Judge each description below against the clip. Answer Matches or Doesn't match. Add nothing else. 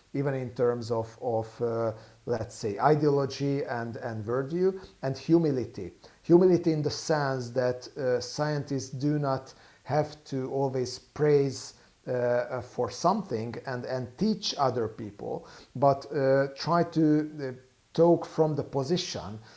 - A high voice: Doesn't match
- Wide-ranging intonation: Doesn't match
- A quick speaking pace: Doesn't match